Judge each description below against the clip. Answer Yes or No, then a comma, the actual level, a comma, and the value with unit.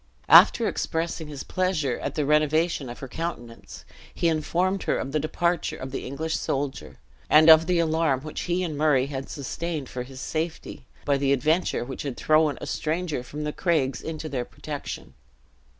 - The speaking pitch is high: No, medium, 155 Hz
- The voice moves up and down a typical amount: Yes, average, 3.2 semitones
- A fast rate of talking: No, average, 180 wpm